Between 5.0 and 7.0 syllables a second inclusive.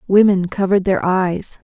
No: 4.8 syllables/s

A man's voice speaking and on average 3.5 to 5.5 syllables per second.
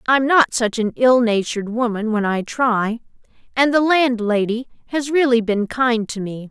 No: female; 4.5 syllables/s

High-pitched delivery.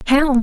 Yes: very high, 265 Hz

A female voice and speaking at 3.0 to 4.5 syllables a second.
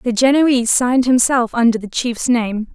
No: female; 4.9 syllables/s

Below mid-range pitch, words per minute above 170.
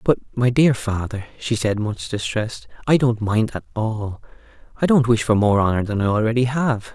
Yes: low, 115 Hz; average, 200 wpm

